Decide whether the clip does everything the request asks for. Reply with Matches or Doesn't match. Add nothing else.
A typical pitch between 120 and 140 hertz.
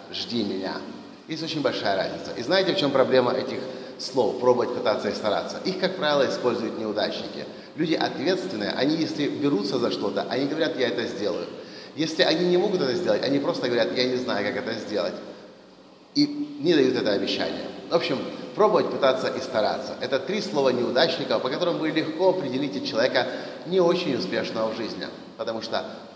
Doesn't match